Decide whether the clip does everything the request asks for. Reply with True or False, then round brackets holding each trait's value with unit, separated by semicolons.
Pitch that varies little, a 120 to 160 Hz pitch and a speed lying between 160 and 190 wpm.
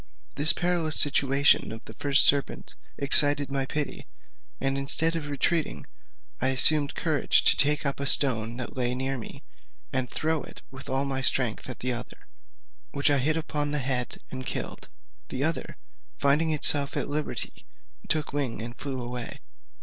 True (2.3 semitones; 140 Hz; 170 wpm)